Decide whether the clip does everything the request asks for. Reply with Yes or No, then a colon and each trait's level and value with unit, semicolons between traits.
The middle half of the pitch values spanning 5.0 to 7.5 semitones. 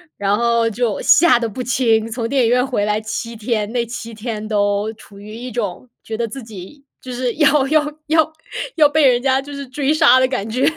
No: average, 3.5 semitones